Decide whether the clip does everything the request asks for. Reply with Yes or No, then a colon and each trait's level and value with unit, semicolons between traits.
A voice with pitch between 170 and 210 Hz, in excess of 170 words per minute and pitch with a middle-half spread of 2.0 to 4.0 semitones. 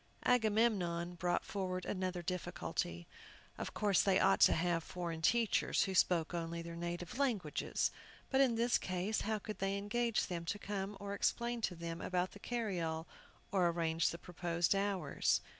No: medium, 185 Hz; average, 160 wpm; average, 3.4 semitones